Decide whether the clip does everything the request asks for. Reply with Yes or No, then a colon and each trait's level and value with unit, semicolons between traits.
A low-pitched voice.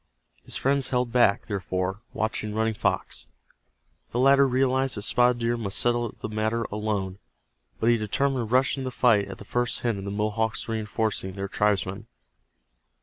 Yes: low, 110 Hz